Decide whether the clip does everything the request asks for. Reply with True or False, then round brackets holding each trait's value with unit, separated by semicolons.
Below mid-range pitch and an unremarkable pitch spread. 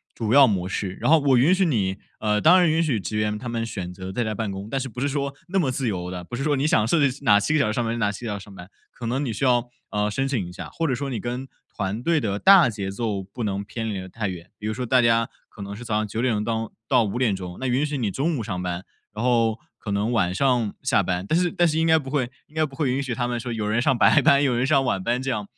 True (115 Hz; 4.7 semitones)